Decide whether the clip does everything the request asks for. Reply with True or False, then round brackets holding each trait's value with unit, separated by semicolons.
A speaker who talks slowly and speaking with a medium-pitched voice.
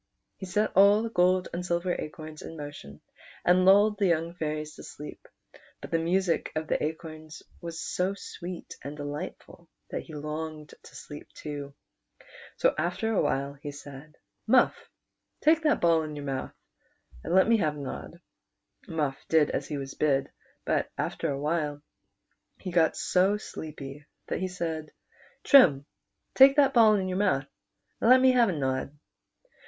False (170 wpm; 160 Hz)